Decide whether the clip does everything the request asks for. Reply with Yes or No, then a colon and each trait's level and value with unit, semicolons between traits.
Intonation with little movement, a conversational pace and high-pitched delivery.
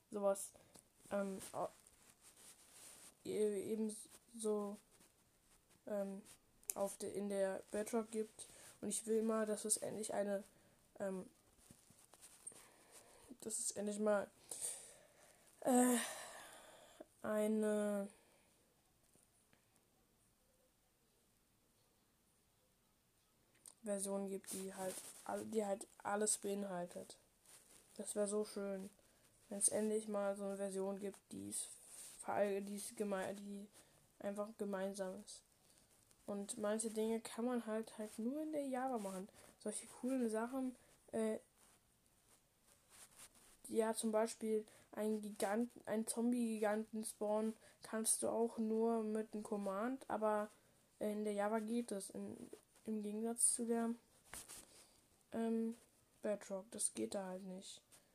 No: narrow, 1.9 semitones; slow, 105 wpm; high, 210 Hz